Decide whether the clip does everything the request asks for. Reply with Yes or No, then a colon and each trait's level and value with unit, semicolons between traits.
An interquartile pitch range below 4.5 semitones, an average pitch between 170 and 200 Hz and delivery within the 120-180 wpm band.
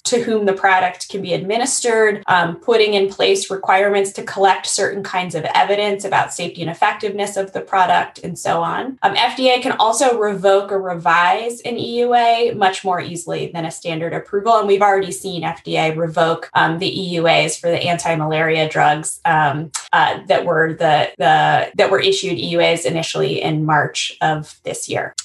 Yes: average, 4.0 semitones; high, 190 Hz; average, 175 wpm